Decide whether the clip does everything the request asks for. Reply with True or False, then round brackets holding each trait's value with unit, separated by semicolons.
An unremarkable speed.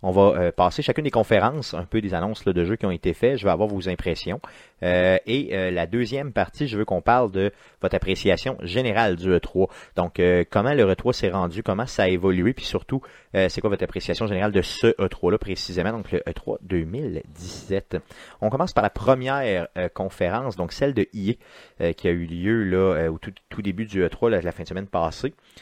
False (225 wpm)